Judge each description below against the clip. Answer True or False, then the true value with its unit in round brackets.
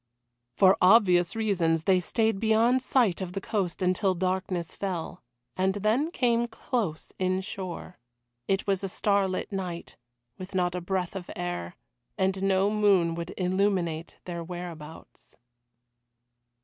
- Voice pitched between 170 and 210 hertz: True (190 Hz)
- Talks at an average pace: False (130 wpm)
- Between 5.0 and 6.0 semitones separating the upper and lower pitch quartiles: False (2.4 semitones)